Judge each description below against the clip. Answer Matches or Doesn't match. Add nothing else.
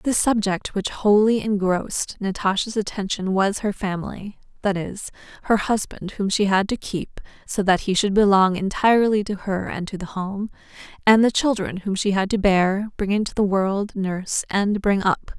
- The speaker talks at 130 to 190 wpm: Matches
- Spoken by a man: Doesn't match